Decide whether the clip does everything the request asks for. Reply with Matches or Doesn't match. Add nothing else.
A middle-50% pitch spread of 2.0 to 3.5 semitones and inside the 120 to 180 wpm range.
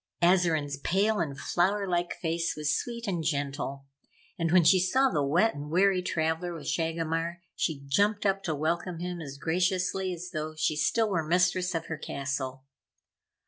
Matches